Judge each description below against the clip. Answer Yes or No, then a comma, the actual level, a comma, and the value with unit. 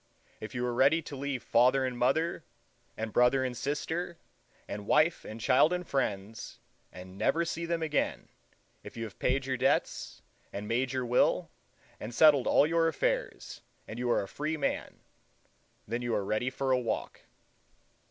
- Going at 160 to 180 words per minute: Yes, average, 165 wpm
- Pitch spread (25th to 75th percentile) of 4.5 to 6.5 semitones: Yes, average, 4.9 semitones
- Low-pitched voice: Yes, low, 130 Hz